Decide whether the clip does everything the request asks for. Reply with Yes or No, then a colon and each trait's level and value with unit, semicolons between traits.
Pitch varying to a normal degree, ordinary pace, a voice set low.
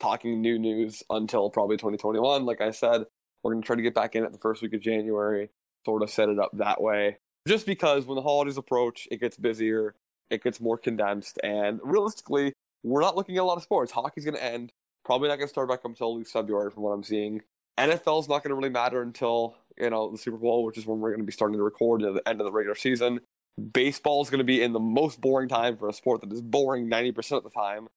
No: average, 3.4 semitones; fast, 245 wpm; low, 115 Hz